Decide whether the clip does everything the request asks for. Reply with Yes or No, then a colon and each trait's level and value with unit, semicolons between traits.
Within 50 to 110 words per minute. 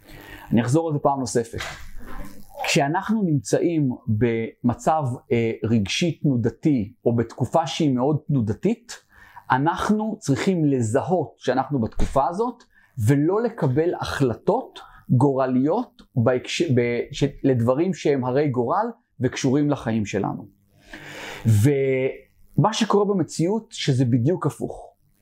Yes: slow, 100 wpm